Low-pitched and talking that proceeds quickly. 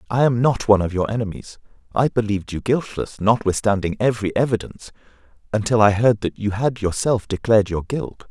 No: low, 110 Hz; average, 175 wpm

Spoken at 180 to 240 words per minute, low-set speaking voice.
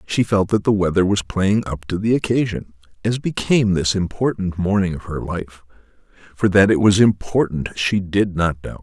Yes: average, 190 wpm; very low, 95 Hz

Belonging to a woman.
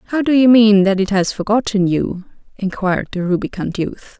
Yes: female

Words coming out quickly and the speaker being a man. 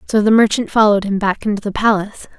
No: fast, 225 wpm; female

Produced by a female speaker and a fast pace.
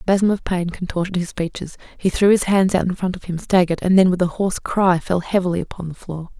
Yes: female; fast, 265 wpm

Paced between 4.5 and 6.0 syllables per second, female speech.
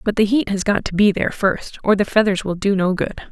Yes: 5.9 syllables/s; female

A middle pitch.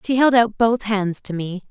No: high, 215 Hz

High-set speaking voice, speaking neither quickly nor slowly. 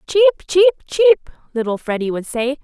Yes: very high, 305 Hz; average, 160 wpm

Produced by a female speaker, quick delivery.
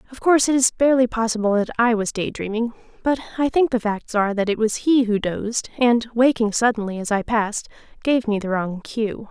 Yes: female; fast, 215 wpm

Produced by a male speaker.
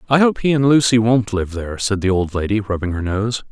Yes: male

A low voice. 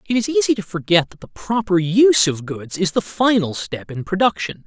No: high, 190 Hz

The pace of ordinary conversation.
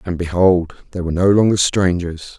Yes: average, 175 wpm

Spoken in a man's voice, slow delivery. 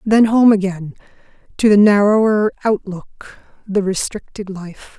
No: female; slow, 120 wpm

